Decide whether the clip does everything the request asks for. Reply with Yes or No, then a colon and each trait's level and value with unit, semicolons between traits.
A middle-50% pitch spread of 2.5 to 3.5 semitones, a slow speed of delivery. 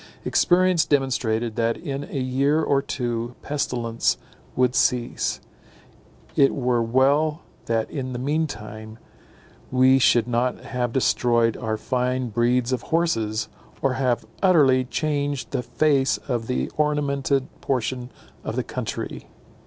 Yes: average, 2.9 semitones; slow, 130 wpm